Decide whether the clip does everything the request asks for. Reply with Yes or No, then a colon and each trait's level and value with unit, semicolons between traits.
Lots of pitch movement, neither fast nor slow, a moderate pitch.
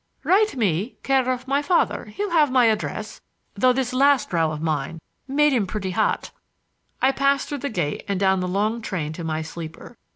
No: wide, 7.2 semitones; average, 190 wpm; high, 225 Hz